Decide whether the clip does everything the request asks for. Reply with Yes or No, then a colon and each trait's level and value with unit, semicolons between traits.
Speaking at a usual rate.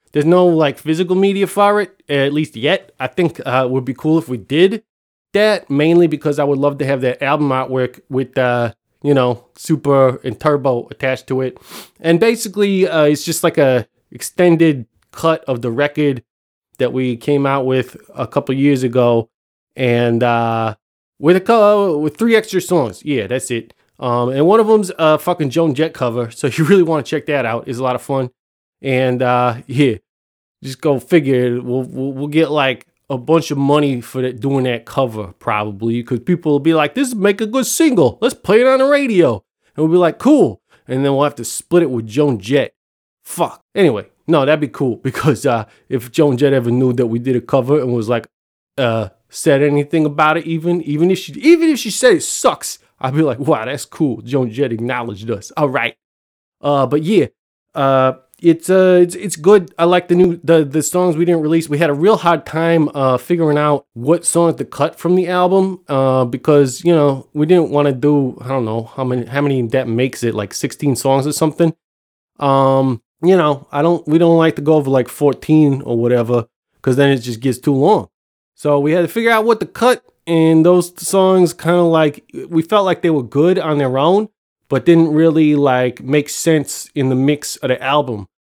No: fast, 215 wpm